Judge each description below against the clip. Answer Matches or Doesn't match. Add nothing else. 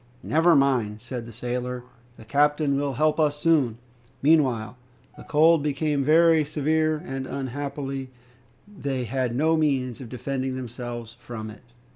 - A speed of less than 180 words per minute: Matches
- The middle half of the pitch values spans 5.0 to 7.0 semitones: Doesn't match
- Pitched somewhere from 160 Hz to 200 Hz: Doesn't match